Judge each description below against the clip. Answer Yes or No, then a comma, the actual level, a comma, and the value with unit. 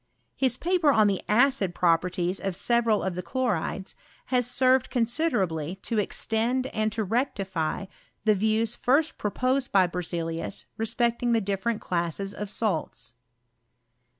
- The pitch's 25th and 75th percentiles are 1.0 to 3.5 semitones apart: No, average, 4.8 semitones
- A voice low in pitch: No, high, 215 Hz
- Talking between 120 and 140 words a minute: Yes, slow, 135 wpm